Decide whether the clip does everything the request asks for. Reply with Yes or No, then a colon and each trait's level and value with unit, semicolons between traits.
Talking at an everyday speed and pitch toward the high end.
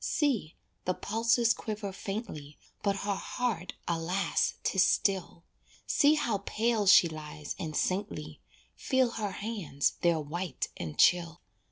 No: slow, 130 wpm; high, 195 Hz